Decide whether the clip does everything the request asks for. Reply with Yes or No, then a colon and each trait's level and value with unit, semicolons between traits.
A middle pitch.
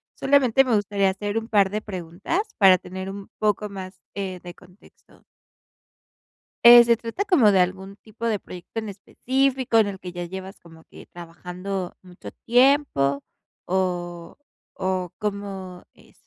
No: high, 195 Hz